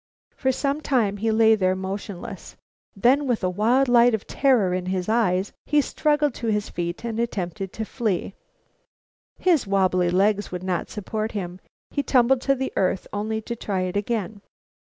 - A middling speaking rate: Yes, average, 175 wpm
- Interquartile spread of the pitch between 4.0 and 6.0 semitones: Yes, average, 4.4 semitones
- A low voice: No, high, 215 Hz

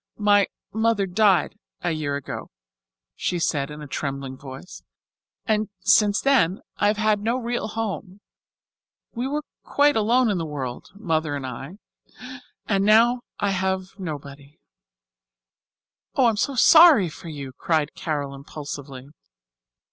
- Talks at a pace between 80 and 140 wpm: Yes, slow, 135 wpm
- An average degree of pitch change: No, wide, 7.0 semitones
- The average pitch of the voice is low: No, high, 190 Hz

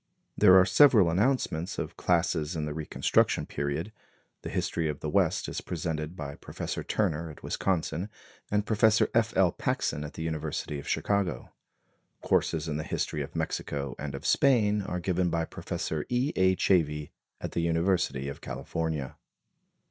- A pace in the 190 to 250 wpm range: No, average, 160 wpm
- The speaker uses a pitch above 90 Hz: No, very low, 85 Hz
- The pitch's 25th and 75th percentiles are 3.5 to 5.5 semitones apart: Yes, average, 4.1 semitones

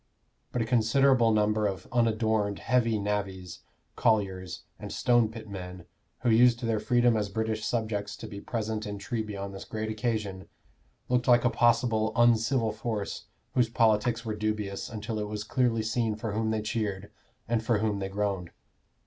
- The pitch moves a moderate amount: No, narrow, 2.0 semitones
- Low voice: Yes, low, 110 Hz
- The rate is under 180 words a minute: Yes, average, 165 wpm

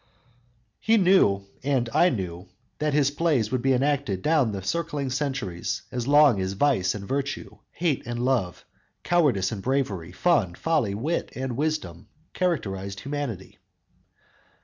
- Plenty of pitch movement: Yes, wide, 7.0 semitones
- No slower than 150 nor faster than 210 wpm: No, average, 140 wpm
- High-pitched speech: No, low, 130 Hz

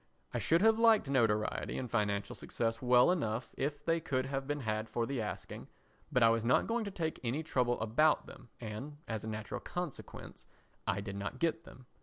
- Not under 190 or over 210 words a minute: Yes, average, 200 wpm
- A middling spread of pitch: No, wide, 5.7 semitones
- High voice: No, low, 125 Hz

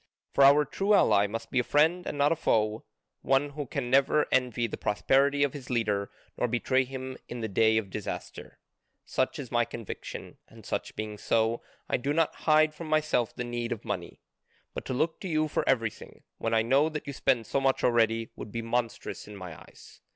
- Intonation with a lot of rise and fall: No, average, 4.2 semitones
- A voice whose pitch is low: Yes, low, 125 Hz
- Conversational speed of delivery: No, fast, 210 wpm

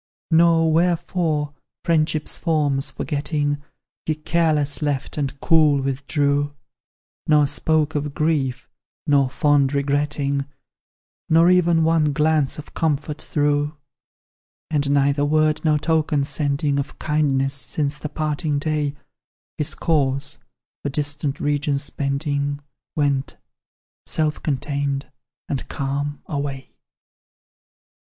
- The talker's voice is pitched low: No, medium, 145 Hz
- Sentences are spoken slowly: Yes, slow, 105 wpm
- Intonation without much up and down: Yes, narrow, 1.6 semitones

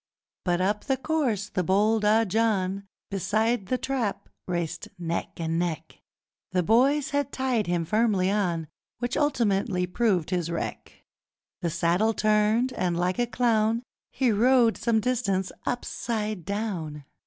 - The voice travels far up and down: No, average, 4.6 semitones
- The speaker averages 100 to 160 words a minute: Yes, average, 140 wpm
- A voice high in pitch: Yes, high, 210 Hz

